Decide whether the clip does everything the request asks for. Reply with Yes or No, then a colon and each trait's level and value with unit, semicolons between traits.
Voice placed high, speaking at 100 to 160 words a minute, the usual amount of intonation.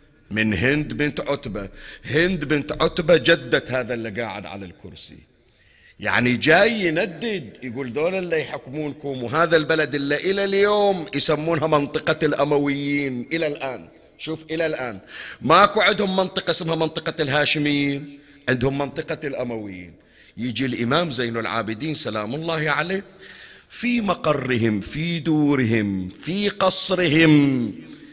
No: medium, 150 Hz; average, 115 wpm; average, 4.9 semitones